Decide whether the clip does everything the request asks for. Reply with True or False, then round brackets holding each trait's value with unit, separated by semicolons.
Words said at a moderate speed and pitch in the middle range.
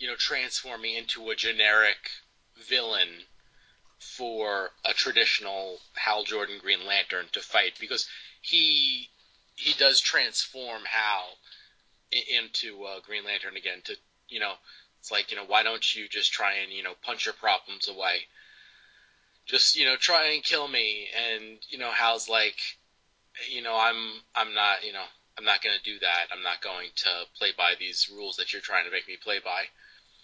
False (175 wpm; 115 Hz)